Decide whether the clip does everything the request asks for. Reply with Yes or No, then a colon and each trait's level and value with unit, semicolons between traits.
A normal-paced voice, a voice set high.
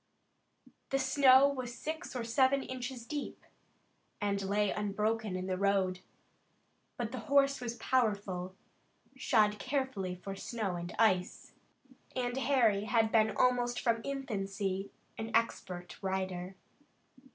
No: slow, 120 wpm; high, 220 Hz